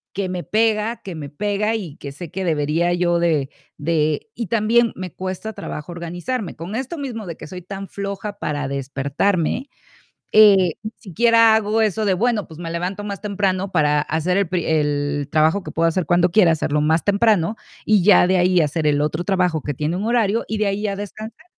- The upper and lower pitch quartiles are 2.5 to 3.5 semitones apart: No, average, 4.6 semitones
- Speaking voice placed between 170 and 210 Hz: Yes, medium, 185 Hz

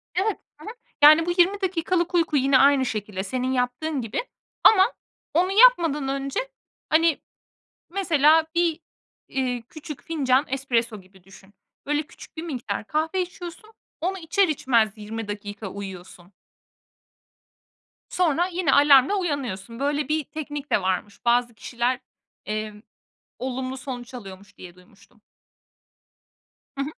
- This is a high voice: Yes, very high, 275 Hz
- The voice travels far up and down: Yes, wide, 6.4 semitones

